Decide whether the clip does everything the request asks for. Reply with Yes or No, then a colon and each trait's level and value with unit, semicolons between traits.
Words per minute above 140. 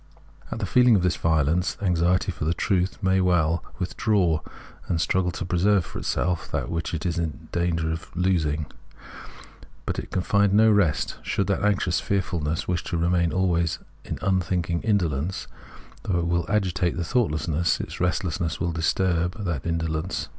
Yes: average, 170 wpm